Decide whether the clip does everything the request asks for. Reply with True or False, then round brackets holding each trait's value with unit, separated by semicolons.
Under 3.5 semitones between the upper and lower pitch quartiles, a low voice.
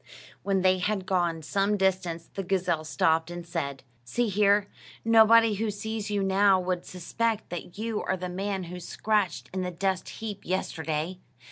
False (2.8 semitones; 190 Hz)